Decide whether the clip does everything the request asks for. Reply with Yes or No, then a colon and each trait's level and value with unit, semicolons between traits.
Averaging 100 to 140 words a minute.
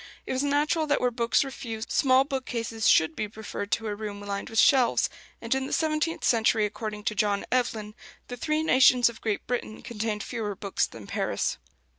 No: average, 195 wpm